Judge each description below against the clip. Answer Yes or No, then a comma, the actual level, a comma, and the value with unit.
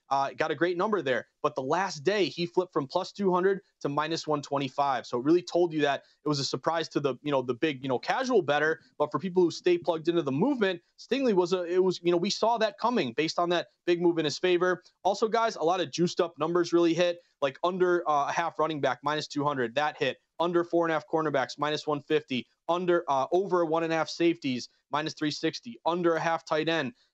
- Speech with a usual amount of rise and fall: Yes, average, 3.0 semitones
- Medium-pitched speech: Yes, medium, 165 Hz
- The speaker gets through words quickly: Yes, fast, 245 wpm